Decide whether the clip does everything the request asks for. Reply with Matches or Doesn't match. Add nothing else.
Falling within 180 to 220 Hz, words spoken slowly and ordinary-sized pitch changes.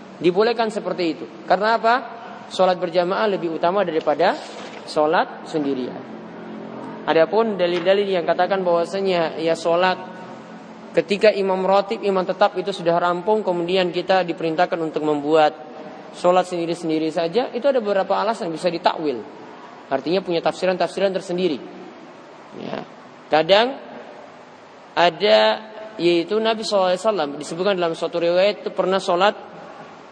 Matches